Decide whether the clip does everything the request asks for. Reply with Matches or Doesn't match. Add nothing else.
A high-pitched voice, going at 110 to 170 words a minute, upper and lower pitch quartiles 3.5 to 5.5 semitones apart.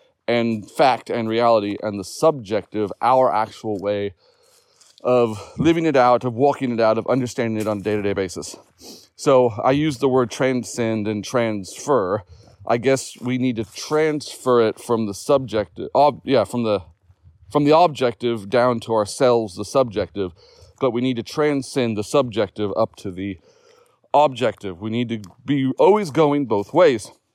Doesn't match